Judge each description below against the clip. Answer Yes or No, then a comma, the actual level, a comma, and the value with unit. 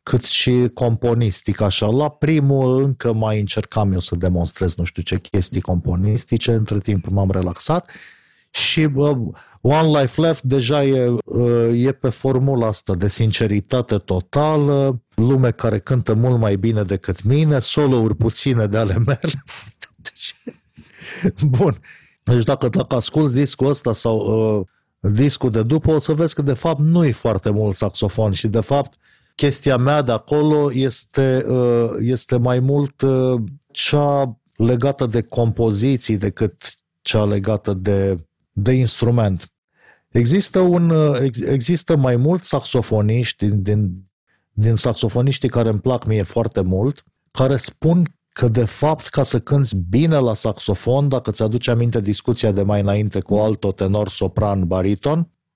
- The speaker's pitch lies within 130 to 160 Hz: No, low, 120 Hz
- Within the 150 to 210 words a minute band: No, average, 140 wpm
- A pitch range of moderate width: Yes, average, 4.6 semitones